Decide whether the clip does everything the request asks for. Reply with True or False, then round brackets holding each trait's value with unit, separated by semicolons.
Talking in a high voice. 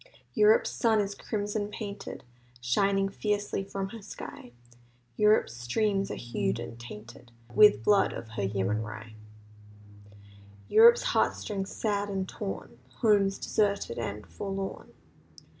True (195 Hz)